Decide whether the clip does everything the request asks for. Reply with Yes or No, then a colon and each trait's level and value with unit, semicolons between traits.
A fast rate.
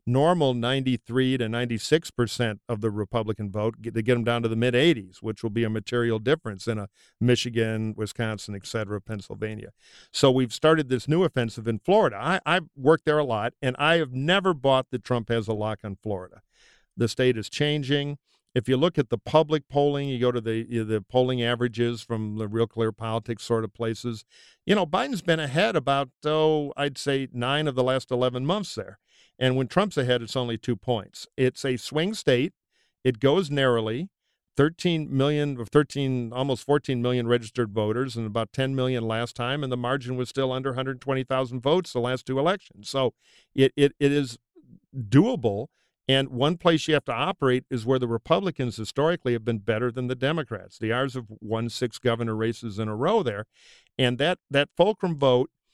No: average, 195 wpm